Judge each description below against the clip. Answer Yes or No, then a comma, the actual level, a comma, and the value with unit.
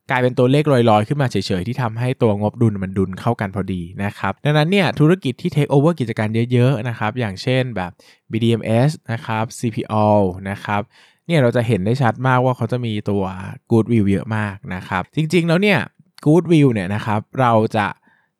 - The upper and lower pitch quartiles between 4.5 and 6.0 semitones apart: No, average, 4.0 semitones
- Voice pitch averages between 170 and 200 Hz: No, low, 115 Hz